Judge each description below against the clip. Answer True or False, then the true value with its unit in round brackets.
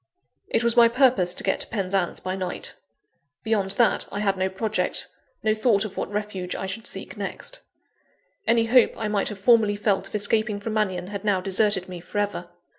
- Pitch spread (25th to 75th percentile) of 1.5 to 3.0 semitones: True (2.5 semitones)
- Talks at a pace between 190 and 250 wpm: True (195 wpm)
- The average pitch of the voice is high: True (205 Hz)